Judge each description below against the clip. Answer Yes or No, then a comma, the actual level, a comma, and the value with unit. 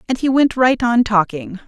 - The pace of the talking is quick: Yes, fast, 215 wpm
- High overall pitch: Yes, high, 230 Hz